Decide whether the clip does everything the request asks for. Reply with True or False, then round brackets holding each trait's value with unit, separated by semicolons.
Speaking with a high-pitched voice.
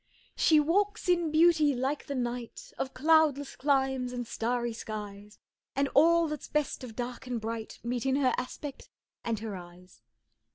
True (260 Hz)